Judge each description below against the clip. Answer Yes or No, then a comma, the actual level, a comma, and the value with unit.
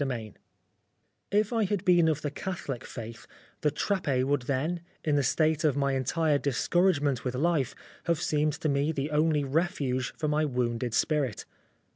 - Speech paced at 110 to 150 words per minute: No, average, 170 wpm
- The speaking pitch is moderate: Yes, medium, 145 Hz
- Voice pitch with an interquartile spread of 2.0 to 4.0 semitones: Yes, average, 3.5 semitones